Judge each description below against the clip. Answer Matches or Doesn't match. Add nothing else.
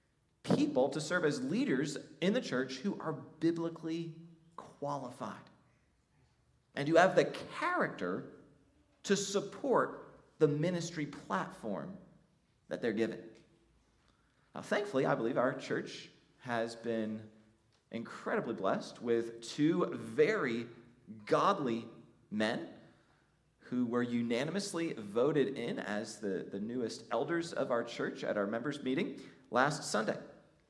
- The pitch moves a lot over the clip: Matches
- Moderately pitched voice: Matches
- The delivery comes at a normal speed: Doesn't match